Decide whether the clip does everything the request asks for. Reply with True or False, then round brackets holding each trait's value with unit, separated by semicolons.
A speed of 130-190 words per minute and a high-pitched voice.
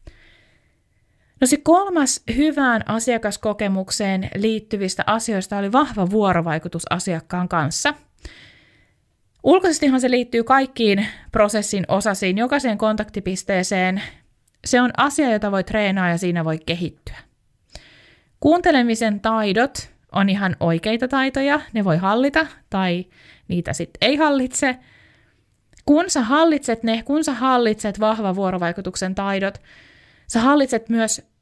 False (105 wpm; 215 Hz)